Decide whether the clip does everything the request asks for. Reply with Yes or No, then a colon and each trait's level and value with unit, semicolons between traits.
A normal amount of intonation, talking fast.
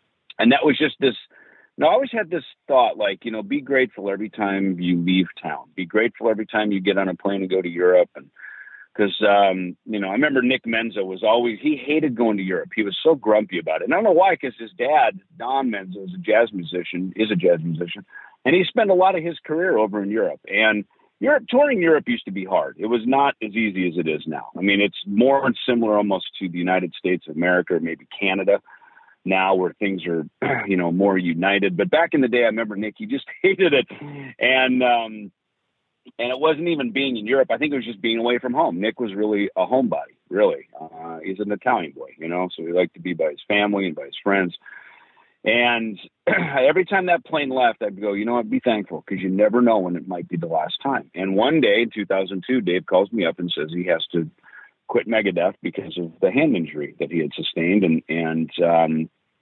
No: wide, 5.8 semitones; fast, 235 wpm